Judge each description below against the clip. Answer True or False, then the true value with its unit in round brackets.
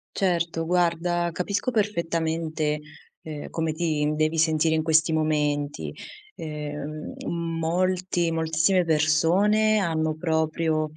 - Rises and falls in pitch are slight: True (1.9 semitones)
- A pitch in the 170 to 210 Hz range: False (160 Hz)